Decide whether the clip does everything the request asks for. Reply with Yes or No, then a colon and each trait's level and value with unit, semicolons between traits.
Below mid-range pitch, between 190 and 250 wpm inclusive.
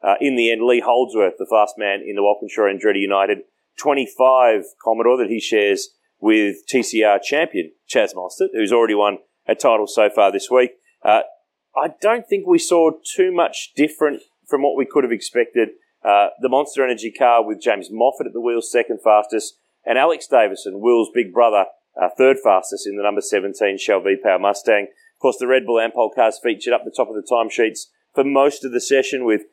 Yes: low, 130 Hz; average, 195 wpm